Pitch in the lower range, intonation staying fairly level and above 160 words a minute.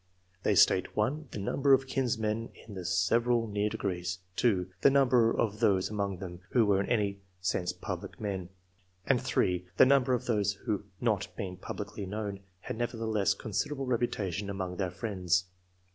No: low, 105 Hz; average, 3.7 semitones; average, 180 wpm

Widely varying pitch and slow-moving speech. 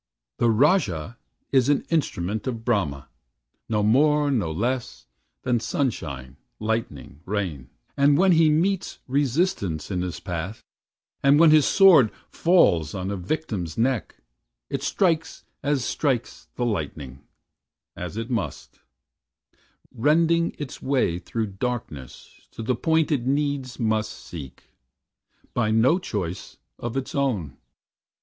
Yes: wide, 7.6 semitones; slow, 125 wpm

